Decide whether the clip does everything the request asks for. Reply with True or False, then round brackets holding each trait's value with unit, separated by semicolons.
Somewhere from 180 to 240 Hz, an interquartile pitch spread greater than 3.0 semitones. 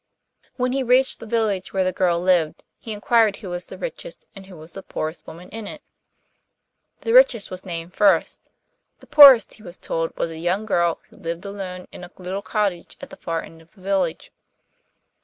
True (190 Hz; 4.2 semitones)